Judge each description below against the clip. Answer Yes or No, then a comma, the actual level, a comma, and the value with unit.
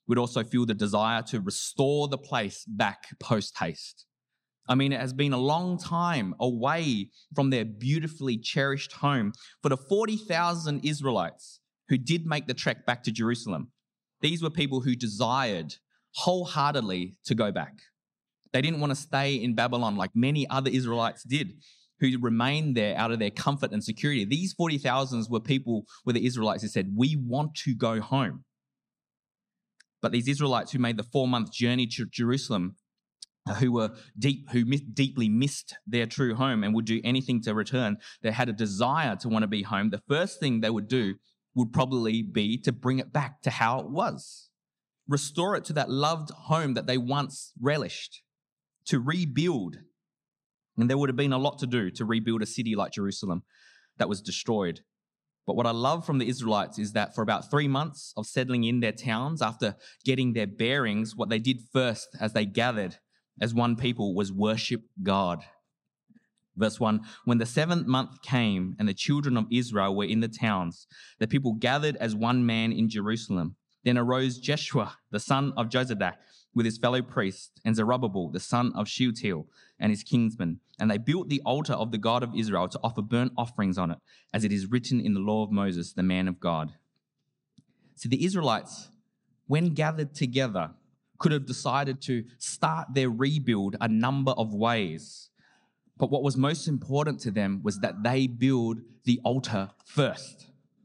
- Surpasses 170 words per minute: Yes, average, 180 wpm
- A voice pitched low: Yes, low, 125 Hz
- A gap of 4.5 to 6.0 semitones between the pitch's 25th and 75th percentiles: No, average, 3.7 semitones